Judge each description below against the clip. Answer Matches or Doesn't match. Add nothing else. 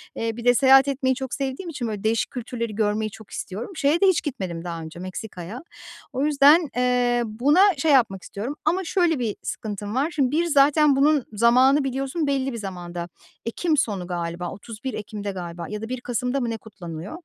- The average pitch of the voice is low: Doesn't match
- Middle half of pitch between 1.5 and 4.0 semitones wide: Doesn't match